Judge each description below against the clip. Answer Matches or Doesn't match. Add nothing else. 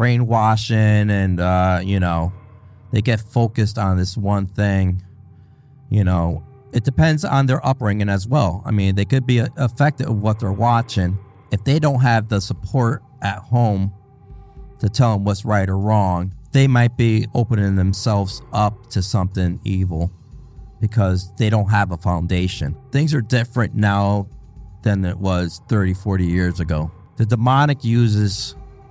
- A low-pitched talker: Matches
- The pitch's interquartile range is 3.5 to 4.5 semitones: Matches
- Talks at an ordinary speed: Matches